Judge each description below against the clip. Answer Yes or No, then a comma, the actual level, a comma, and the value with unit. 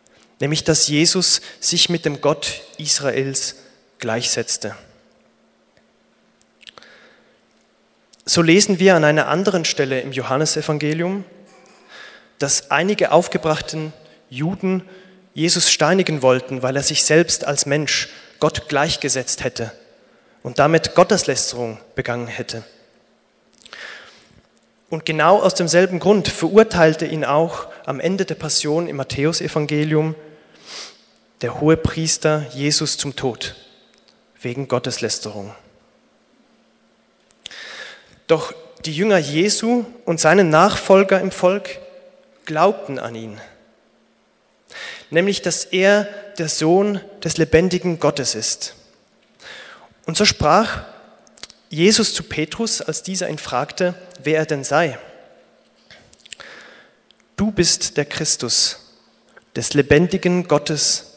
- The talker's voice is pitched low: No, medium, 155 Hz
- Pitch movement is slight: No, average, 4.2 semitones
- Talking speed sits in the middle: No, slow, 100 wpm